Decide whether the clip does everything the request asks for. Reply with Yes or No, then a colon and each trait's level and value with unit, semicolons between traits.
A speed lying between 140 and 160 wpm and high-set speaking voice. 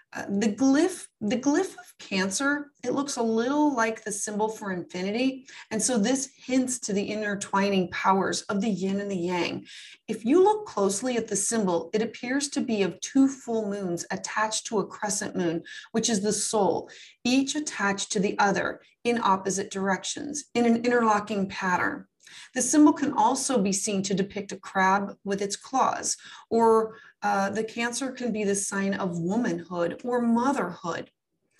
No: average, 175 wpm; high, 220 Hz